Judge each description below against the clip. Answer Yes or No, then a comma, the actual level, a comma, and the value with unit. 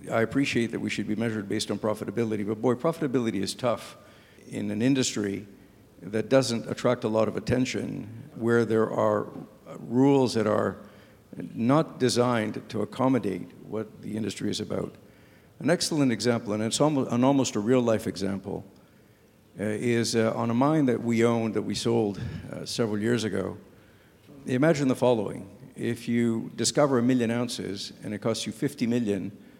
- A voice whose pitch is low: Yes, low, 115 Hz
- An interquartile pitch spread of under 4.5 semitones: Yes, average, 2.7 semitones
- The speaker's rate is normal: Yes, average, 160 wpm